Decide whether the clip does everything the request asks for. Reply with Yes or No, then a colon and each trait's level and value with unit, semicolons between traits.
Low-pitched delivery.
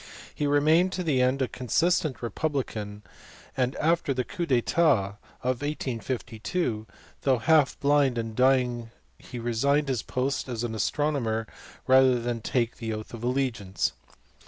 Yes: low, 130 Hz